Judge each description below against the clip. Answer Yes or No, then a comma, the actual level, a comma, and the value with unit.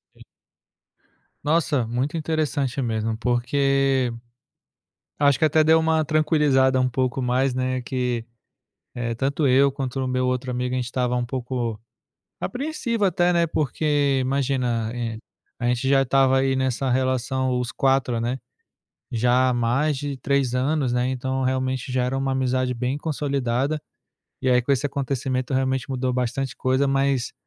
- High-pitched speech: No, low, 130 Hz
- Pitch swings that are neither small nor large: No, narrow, 1.9 semitones